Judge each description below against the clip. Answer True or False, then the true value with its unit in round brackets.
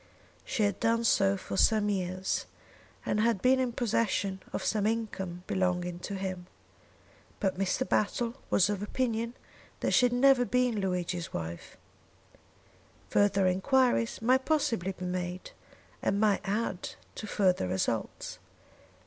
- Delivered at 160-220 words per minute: False (135 wpm)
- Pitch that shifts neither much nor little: True (3.9 semitones)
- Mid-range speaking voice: False (205 Hz)